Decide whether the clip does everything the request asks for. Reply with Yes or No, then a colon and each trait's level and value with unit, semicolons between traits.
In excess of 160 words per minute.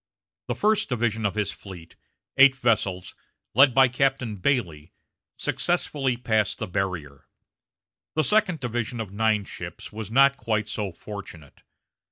No: slow, 135 wpm